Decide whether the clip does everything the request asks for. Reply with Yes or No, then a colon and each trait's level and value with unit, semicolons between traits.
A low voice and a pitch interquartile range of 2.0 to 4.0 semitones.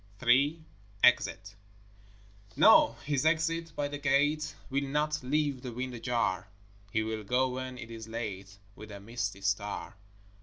No: low, 125 Hz; average, 4.8 semitones